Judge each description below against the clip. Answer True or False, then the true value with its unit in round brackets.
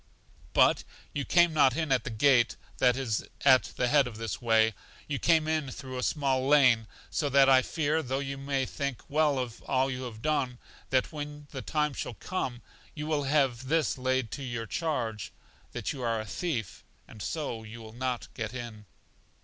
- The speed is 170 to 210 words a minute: True (195 wpm)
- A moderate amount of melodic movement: True (3.5 semitones)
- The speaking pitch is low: True (130 Hz)